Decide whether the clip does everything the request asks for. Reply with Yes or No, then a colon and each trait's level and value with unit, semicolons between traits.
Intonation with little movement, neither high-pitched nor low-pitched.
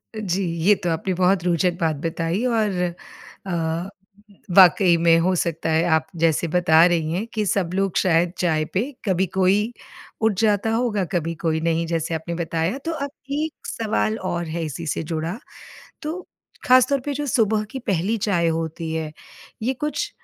No: average, 4.4 semitones; medium, 180 Hz